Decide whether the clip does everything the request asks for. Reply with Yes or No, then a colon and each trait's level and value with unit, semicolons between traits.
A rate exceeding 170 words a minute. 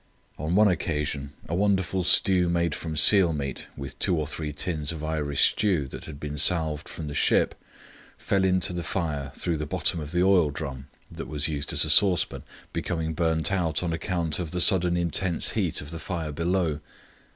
Yes: average, 195 wpm